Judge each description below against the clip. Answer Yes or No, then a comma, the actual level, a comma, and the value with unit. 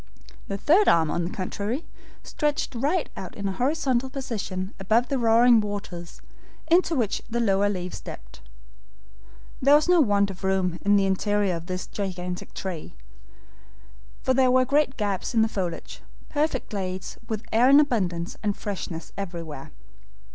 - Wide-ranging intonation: Yes, wide, 5.7 semitones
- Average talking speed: Yes, average, 155 wpm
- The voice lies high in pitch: Yes, high, 205 Hz